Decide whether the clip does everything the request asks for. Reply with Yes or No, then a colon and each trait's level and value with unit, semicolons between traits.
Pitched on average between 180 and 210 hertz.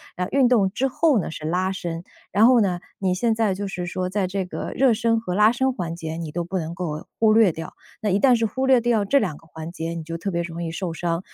Yes: high, 190 Hz